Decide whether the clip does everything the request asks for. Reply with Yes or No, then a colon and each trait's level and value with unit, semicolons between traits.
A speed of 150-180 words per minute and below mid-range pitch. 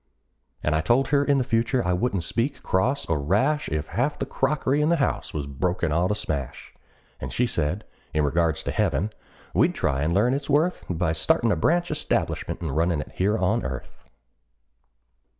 No: average, 190 wpm; very low, 95 Hz